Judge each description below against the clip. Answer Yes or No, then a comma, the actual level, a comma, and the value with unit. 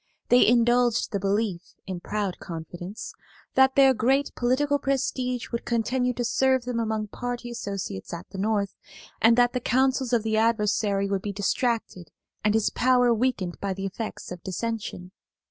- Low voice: No, high, 225 Hz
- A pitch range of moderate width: Yes, average, 3.9 semitones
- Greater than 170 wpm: No, average, 165 wpm